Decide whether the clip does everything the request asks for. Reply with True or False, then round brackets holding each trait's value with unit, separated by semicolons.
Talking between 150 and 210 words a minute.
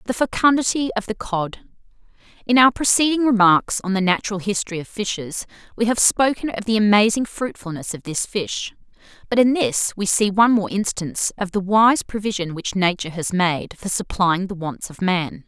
True (180 wpm)